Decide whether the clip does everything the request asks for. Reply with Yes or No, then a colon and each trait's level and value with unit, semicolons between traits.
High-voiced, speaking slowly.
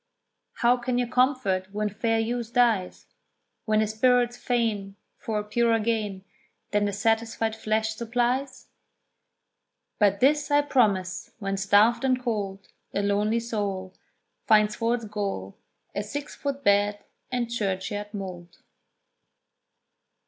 Yes: high, 220 Hz; slow, 125 wpm